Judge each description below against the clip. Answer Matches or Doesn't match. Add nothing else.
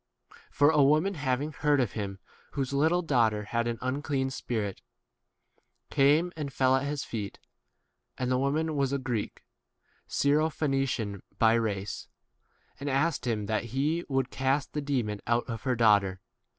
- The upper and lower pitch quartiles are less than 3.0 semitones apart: Doesn't match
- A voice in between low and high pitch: Doesn't match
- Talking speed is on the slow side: Doesn't match